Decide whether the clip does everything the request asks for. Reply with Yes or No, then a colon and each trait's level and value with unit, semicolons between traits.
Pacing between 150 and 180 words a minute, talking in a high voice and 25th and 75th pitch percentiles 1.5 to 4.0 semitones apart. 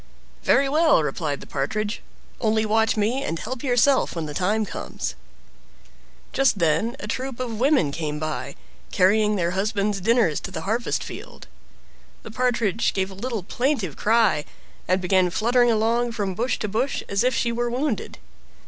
No: average, 165 wpm; high, 215 Hz; average, 4.6 semitones